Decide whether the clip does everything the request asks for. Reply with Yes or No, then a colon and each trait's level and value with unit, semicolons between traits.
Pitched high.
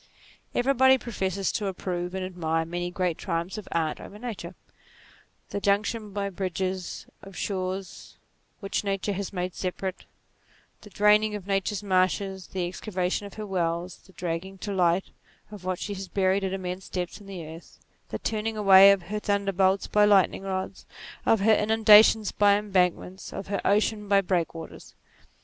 Yes: high, 195 Hz